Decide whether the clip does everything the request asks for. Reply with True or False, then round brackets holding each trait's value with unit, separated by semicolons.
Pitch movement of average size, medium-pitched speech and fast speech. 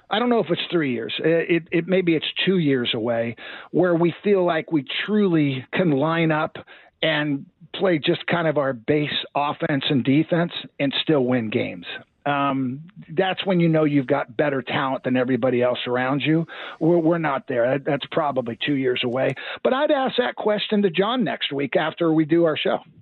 False (4.1 semitones; 155 Hz; 195 wpm)